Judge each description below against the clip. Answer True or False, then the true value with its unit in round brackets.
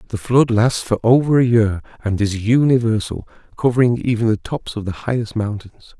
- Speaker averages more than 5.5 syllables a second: False (5.2 syllables/s)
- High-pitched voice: False (115 Hz)